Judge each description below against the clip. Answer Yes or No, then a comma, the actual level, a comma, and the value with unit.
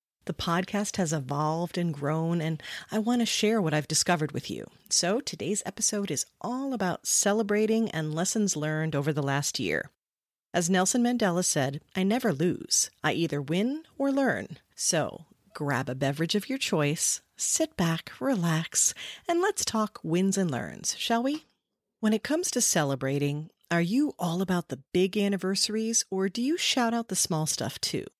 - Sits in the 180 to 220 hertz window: Yes, medium, 185 Hz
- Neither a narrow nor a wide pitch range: No, wide, 6.0 semitones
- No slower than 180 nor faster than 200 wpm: No, average, 170 wpm